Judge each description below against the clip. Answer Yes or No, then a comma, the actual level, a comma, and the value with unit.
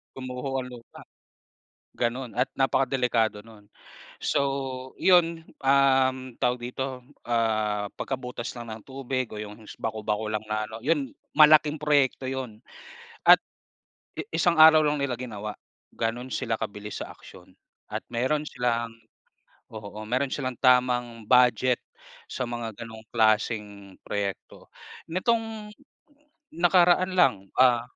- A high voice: No, low, 125 Hz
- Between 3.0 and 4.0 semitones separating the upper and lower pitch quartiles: Yes, average, 3.5 semitones